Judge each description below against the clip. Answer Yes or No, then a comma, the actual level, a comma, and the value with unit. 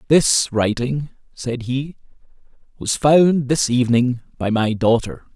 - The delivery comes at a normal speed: No, slow, 125 wpm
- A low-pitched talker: Yes, low, 130 Hz